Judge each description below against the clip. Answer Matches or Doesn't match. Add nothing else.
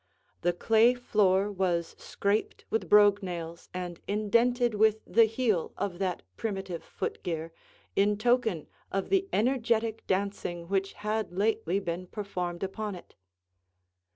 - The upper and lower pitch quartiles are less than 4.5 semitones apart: Matches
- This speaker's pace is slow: Matches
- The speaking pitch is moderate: Doesn't match